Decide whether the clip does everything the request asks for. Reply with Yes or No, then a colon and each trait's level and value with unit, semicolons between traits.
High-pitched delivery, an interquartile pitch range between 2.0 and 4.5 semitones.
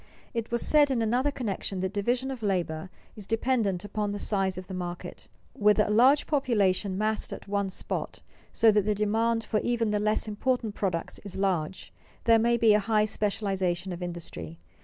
Yes: high, 210 Hz; average, 3.2 semitones